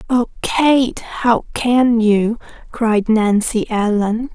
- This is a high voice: Yes, high, 230 Hz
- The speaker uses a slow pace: Yes, slow, 110 wpm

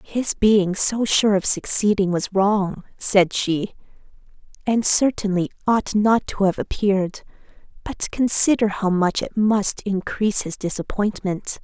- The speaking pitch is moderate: No, high, 200 Hz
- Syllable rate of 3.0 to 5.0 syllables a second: Yes, 4.0 syllables/s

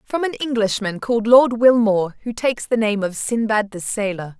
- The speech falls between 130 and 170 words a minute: No, average, 190 wpm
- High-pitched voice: Yes, high, 220 Hz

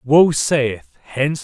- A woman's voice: No, male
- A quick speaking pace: No, slow, 125 wpm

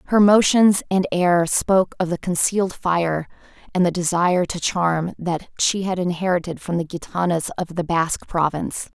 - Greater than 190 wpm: No, average, 165 wpm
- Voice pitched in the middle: Yes, medium, 175 Hz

